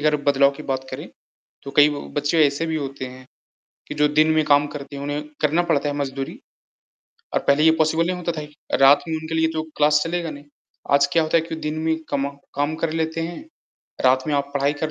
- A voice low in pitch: No, medium, 150 Hz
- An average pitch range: No, narrow, 2.1 semitones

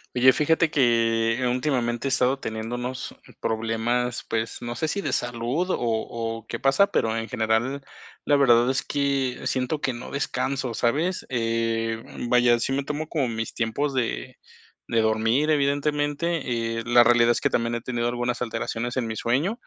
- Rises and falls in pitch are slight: No, average, 3.2 semitones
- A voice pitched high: No, low, 120 Hz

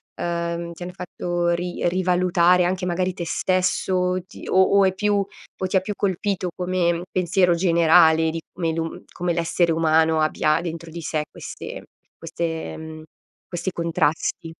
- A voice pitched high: No, medium, 175 Hz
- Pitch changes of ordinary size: No, narrow, 1.8 semitones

